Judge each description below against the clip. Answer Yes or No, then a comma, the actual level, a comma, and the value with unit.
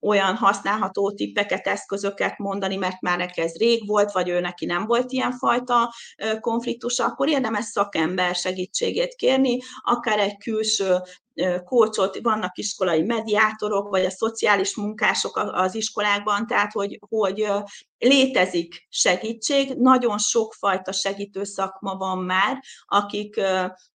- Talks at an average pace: Yes, average, 125 wpm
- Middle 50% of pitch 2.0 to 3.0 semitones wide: No, average, 3.5 semitones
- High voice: Yes, high, 205 Hz